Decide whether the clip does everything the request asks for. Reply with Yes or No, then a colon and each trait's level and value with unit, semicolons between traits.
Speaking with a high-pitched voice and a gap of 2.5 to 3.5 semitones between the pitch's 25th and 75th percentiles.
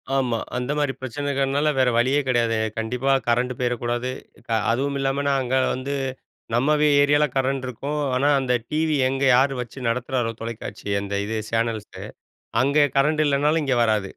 No: low, 130 Hz; average, 2.8 semitones